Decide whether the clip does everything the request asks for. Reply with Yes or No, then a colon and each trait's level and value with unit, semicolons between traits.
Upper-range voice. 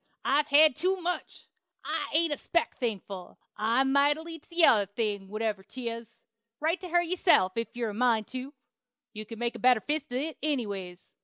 Yes: very high, 255 Hz